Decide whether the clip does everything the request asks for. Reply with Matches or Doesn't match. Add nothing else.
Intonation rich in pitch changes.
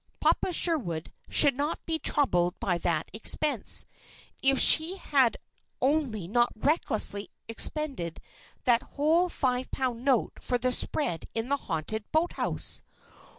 Matches